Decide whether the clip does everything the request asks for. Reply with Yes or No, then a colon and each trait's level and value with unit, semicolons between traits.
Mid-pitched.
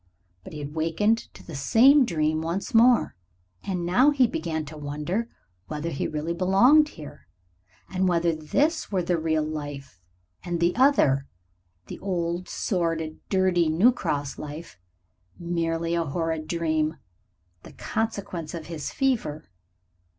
Yes: medium, 170 Hz